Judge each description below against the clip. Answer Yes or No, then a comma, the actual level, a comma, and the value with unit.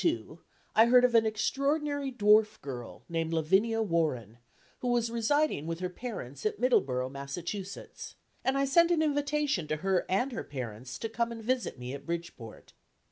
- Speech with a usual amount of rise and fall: No, wide, 8.6 semitones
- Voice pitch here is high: Yes, high, 215 Hz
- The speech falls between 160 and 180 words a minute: Yes, average, 175 wpm